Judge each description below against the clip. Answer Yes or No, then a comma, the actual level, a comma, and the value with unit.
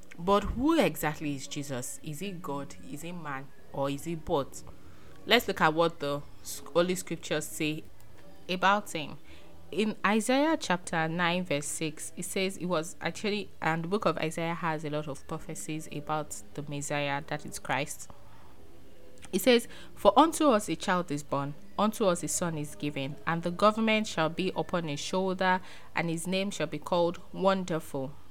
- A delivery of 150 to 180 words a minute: Yes, average, 175 wpm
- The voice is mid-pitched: Yes, medium, 160 Hz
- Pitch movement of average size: Yes, average, 4.1 semitones